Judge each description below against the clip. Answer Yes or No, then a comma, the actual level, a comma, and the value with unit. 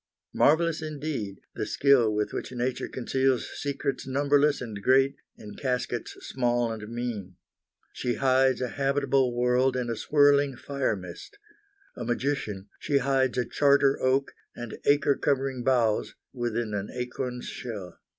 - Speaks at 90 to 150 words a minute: Yes, average, 140 wpm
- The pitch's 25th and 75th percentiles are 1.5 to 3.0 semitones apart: Yes, narrow, 2.6 semitones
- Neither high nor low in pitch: No, low, 130 Hz